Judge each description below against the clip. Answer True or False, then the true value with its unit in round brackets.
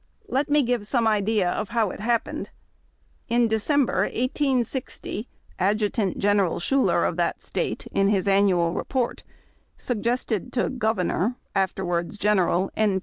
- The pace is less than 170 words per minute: True (140 wpm)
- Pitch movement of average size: True (3.9 semitones)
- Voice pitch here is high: True (215 Hz)